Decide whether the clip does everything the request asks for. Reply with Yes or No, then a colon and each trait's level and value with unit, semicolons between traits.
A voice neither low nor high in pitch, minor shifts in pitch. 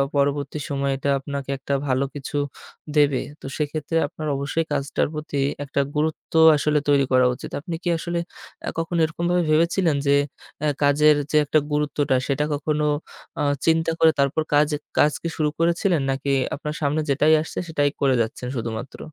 Yes: medium, 150 Hz; narrow, 2.2 semitones